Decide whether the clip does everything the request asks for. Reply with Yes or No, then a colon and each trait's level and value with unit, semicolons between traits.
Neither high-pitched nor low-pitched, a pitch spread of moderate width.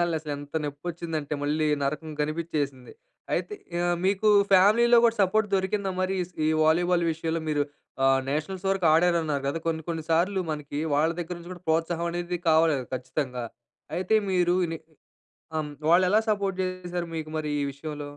Yes: medium, 165 Hz; average, 3.2 semitones